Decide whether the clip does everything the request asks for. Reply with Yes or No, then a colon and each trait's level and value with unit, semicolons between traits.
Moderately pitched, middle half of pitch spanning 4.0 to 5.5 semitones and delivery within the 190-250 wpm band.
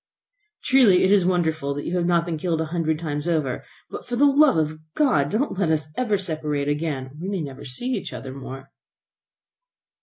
Yes: medium, 160 Hz; average, 4.4 semitones; fast, 205 wpm